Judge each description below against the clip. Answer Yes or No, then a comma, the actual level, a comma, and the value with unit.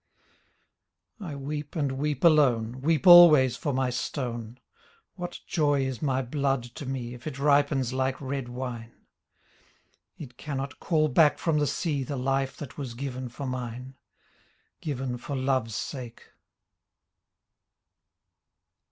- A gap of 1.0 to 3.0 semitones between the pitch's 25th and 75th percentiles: Yes, average, 2.7 semitones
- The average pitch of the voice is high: No, low, 135 Hz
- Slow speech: Yes, slow, 130 wpm